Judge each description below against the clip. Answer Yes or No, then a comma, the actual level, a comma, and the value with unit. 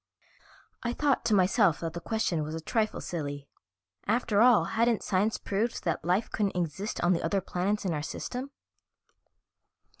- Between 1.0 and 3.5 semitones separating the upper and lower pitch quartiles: No, average, 4.7 semitones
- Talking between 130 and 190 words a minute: Yes, average, 160 wpm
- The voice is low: No, high, 195 Hz